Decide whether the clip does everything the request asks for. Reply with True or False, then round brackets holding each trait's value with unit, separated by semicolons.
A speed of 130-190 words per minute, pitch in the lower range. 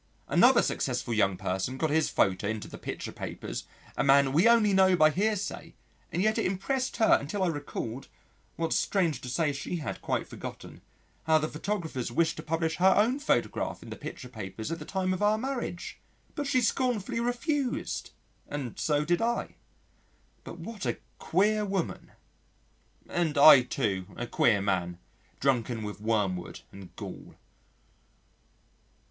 False (160 wpm; 160 Hz)